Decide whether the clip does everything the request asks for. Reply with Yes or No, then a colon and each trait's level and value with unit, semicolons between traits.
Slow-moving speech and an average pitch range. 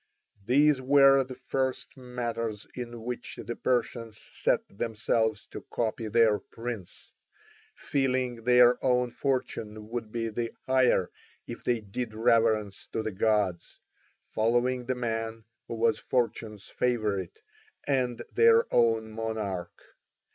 No: slow, 120 wpm; narrow, 2.2 semitones